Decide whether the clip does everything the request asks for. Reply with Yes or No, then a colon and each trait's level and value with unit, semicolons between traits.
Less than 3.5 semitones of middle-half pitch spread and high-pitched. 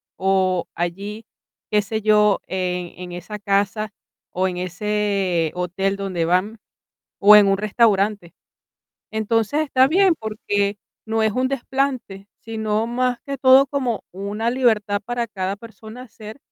Yes: average, 2.9 semitones; high, 210 Hz